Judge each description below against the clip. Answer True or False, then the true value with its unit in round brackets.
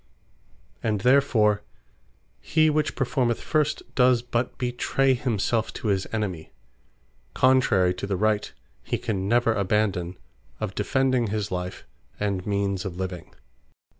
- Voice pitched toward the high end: False (110 Hz)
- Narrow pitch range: False (4.4 semitones)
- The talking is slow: True (125 wpm)